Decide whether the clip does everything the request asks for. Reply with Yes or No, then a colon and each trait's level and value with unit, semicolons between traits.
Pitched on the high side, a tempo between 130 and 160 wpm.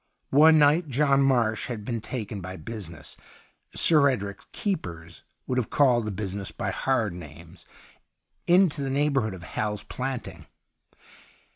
No: low, 120 Hz; average, 155 wpm